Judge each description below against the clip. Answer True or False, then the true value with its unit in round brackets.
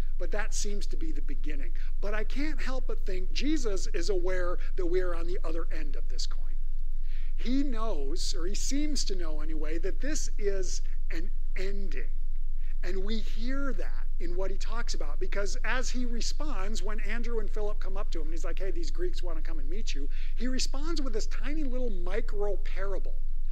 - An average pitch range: False (6.3 semitones)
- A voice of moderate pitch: False (215 Hz)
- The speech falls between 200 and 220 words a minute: True (205 wpm)